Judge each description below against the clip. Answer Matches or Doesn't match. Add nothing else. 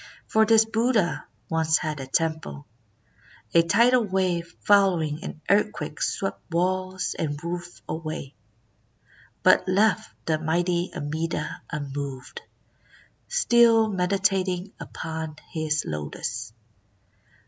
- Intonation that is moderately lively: Matches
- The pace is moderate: Doesn't match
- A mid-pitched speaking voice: Matches